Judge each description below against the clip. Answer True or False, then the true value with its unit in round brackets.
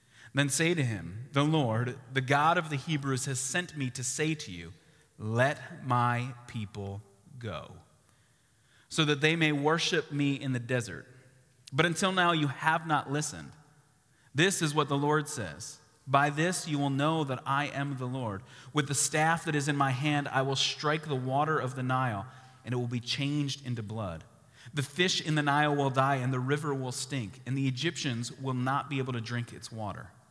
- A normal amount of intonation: True (3.0 semitones)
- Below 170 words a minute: False (200 wpm)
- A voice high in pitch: False (135 Hz)